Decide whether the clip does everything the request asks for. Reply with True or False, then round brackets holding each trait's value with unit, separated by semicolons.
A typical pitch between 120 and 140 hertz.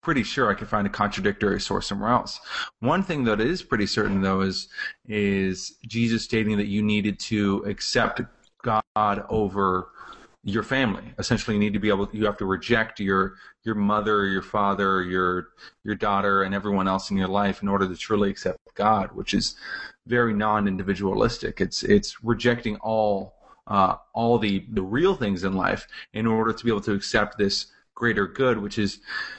False (105 Hz)